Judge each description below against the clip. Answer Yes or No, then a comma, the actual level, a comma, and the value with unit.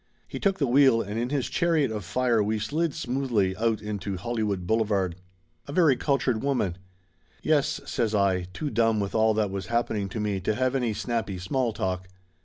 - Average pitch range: Yes, average, 4.5 semitones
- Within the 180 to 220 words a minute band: Yes, average, 190 wpm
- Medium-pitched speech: No, low, 110 Hz